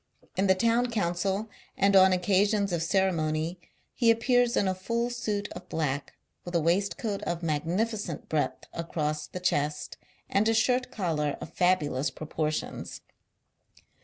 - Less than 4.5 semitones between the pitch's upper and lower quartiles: No, average, 4.8 semitones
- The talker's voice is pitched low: No, medium, 185 Hz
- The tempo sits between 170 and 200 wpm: No, average, 140 wpm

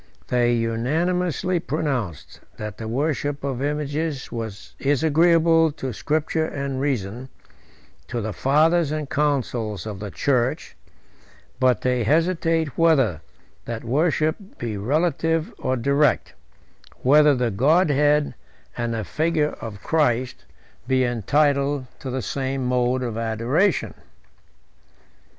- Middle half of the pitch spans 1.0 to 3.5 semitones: No, average, 4.3 semitones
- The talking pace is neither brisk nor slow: No, slow, 115 wpm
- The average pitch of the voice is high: No, medium, 140 Hz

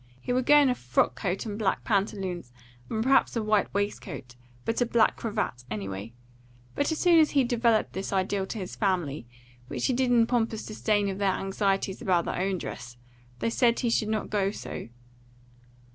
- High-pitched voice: Yes, high, 205 Hz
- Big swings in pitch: No, average, 4.0 semitones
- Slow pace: No, average, 190 wpm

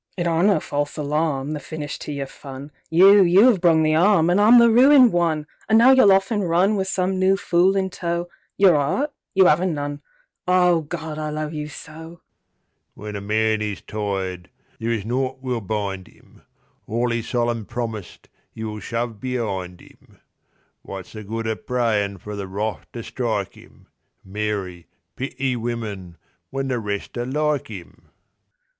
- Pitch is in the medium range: Yes, medium, 145 Hz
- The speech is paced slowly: No, average, 150 wpm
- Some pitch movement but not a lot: No, wide, 8.1 semitones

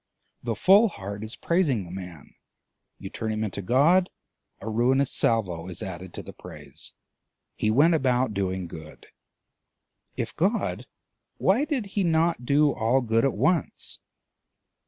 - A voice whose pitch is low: Yes, low, 120 Hz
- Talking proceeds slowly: No, average, 145 wpm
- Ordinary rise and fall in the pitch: No, wide, 8.3 semitones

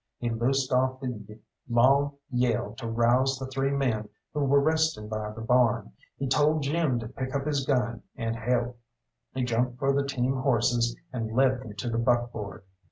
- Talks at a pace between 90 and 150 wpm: No, average, 180 wpm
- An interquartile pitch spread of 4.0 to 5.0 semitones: No, average, 2.7 semitones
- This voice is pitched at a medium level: No, low, 125 Hz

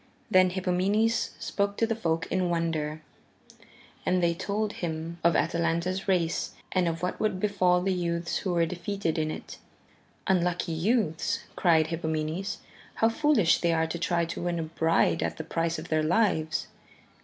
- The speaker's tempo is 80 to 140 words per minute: No, average, 165 wpm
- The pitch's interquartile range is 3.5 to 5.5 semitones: No, narrow, 2.6 semitones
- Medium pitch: Yes, medium, 175 Hz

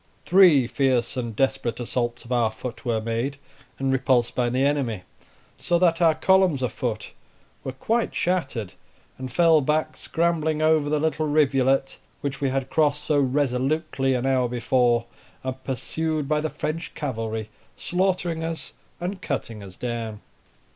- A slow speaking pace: No, average, 155 wpm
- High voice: No, low, 135 Hz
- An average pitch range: Yes, average, 4.4 semitones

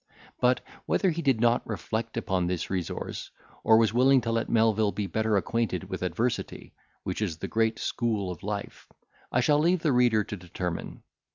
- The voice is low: Yes, low, 110 Hz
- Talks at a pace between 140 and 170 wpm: No, average, 180 wpm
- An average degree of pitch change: Yes, average, 3.3 semitones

